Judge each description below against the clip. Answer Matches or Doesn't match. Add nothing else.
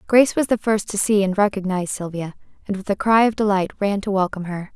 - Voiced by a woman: Matches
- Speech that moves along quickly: Matches